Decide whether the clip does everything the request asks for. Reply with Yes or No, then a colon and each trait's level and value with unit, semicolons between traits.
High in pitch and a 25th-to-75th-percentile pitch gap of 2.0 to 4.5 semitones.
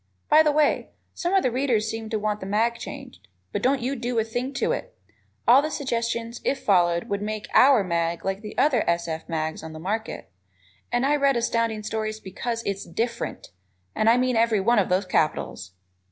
Yes: high, 225 Hz; average, 4.0 semitones